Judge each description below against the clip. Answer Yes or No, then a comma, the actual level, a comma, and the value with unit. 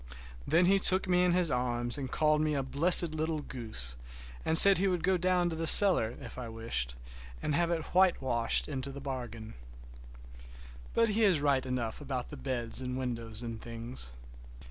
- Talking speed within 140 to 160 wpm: No, average, 175 wpm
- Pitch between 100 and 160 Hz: Yes, medium, 140 Hz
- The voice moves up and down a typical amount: No, wide, 6.4 semitones